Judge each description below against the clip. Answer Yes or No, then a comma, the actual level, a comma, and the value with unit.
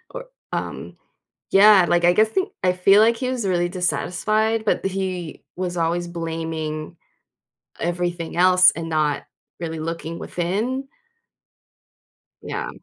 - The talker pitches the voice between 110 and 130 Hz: No, medium, 180 Hz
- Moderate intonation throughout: Yes, average, 3.5 semitones